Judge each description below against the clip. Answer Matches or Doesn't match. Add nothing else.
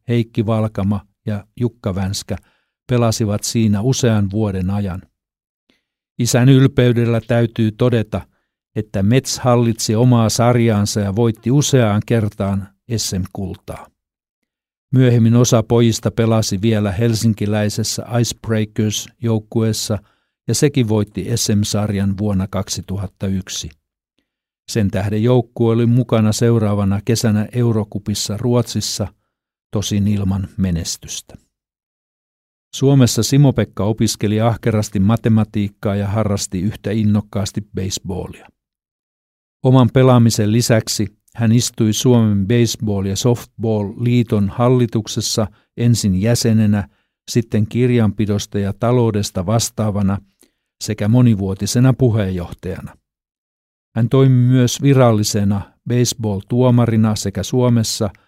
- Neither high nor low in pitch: Doesn't match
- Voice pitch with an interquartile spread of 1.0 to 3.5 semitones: Matches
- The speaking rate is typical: Doesn't match